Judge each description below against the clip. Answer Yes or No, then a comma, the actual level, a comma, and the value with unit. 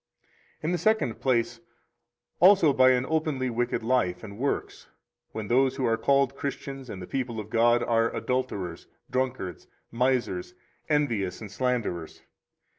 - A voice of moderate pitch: No, low, 125 Hz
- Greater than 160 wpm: No, average, 140 wpm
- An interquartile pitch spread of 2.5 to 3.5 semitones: Yes, average, 3.2 semitones